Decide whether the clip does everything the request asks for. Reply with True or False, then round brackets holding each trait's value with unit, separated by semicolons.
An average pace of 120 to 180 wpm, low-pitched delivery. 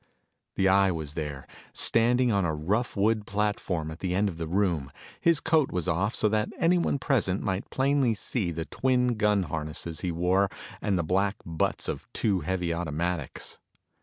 True (175 wpm; 95 Hz)